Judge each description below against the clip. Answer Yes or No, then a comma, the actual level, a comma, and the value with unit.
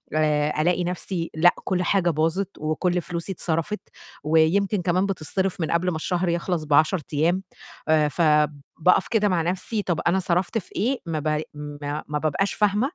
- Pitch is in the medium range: Yes, medium, 170 Hz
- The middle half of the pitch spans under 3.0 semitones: No, average, 3.3 semitones